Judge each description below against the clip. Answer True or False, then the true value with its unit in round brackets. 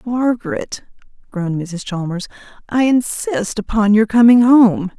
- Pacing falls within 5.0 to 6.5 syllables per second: False (4.2 syllables/s)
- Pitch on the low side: False (215 Hz)